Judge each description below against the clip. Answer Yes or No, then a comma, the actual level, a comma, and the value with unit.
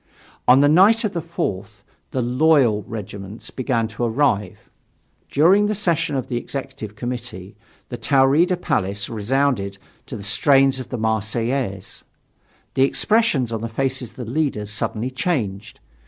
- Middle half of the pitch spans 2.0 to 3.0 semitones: No, average, 4.9 semitones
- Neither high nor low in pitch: No, low, 125 Hz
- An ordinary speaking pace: Yes, average, 145 wpm